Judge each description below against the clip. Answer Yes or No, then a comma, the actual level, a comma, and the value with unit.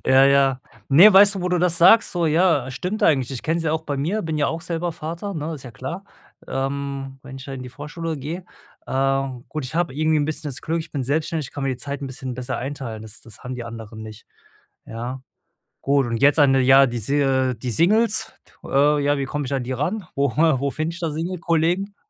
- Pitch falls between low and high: Yes, medium, 145 Hz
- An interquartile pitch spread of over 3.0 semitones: Yes, average, 3.8 semitones